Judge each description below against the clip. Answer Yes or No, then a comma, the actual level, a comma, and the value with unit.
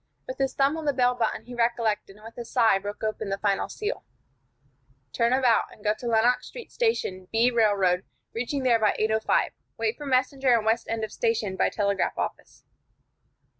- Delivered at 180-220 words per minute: Yes, average, 190 wpm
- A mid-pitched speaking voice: No, high, 230 Hz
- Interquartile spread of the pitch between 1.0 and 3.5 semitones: Yes, average, 3.1 semitones